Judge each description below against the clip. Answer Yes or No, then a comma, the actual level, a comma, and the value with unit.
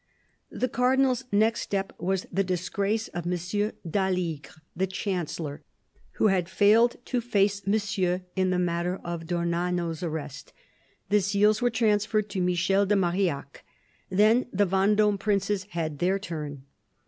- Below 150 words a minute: Yes, slow, 135 wpm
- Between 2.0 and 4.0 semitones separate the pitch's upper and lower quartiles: Yes, average, 3.1 semitones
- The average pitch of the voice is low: No, high, 190 Hz